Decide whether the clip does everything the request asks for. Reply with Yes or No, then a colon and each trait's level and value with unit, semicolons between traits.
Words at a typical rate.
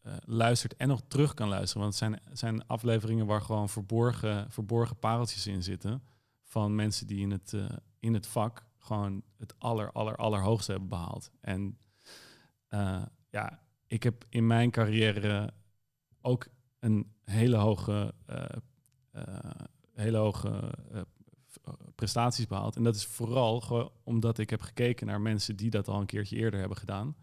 Yes: average, 160 wpm